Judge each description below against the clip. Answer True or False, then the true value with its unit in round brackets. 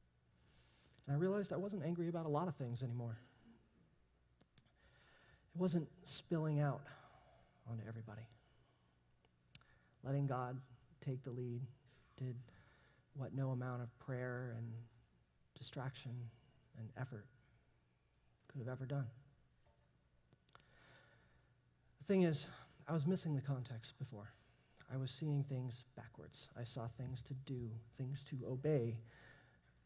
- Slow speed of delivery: True (120 wpm)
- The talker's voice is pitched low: True (125 Hz)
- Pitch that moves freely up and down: False (3.6 semitones)